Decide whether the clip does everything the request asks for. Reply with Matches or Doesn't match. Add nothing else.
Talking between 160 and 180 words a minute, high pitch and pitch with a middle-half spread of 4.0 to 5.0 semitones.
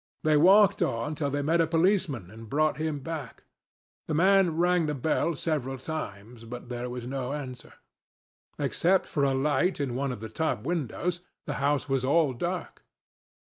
Doesn't match